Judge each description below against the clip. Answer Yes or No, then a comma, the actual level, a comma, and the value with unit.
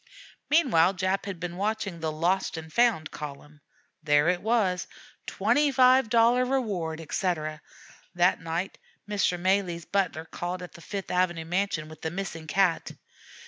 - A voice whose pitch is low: No, medium, 180 Hz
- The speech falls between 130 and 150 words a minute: Yes, average, 140 wpm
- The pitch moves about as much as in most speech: Yes, average, 3.8 semitones